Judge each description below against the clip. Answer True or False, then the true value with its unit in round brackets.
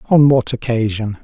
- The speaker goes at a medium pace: True (145 wpm)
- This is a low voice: True (120 Hz)